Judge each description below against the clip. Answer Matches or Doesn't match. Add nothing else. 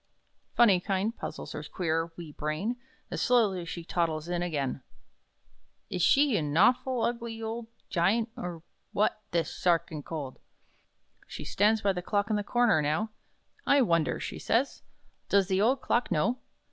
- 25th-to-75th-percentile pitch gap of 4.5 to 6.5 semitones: Matches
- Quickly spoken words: Doesn't match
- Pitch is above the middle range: Matches